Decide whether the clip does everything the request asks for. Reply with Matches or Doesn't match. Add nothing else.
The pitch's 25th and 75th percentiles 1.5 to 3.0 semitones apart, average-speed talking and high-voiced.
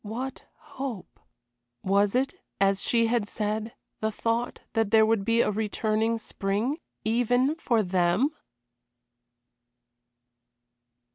Doesn't match